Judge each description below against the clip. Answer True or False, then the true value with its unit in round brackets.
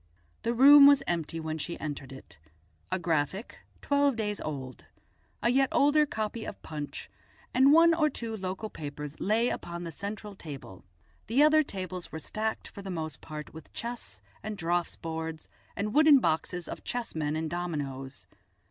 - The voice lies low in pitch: False (185 Hz)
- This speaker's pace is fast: False (165 wpm)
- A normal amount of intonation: False (7.1 semitones)